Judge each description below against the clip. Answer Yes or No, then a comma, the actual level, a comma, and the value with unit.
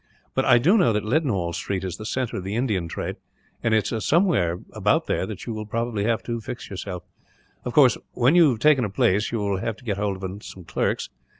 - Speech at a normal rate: No, fast, 225 wpm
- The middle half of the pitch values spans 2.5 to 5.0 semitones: Yes, average, 4.2 semitones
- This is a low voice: Yes, low, 110 Hz